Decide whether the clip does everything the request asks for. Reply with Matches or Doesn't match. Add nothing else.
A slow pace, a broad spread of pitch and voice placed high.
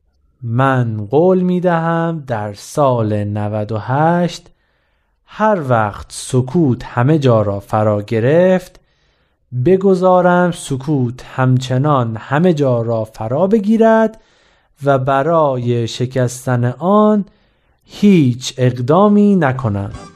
Doesn't match